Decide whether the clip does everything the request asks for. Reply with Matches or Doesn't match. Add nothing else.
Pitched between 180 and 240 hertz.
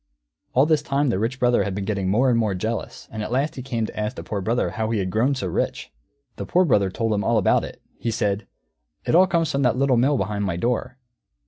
Doesn't match